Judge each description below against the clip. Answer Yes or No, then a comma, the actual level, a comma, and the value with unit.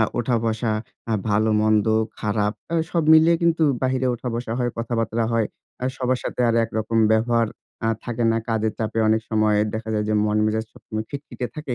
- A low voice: Yes, low, 115 Hz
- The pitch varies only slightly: Yes, narrow, 2.2 semitones